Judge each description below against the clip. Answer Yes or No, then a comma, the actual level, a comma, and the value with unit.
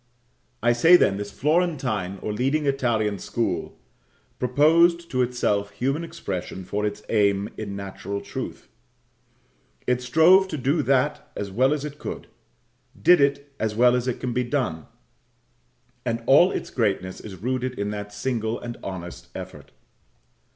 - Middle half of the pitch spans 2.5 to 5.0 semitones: No, wide, 5.4 semitones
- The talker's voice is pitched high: No, low, 125 Hz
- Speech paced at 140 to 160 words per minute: Yes, average, 150 wpm